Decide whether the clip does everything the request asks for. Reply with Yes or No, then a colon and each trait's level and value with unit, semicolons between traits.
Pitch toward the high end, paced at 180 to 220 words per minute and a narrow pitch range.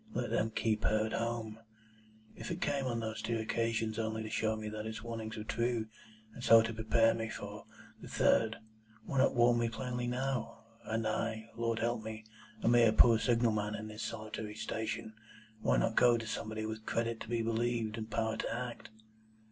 No: low, 115 Hz; average, 195 wpm; narrow, 1.1 semitones